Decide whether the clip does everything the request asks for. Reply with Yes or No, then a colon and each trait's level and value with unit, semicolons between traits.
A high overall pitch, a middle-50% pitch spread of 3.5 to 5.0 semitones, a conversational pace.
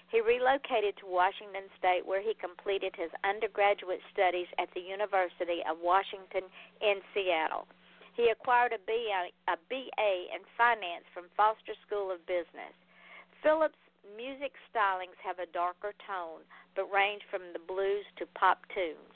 No: high, 195 Hz; average, 2.8 semitones; average, 145 wpm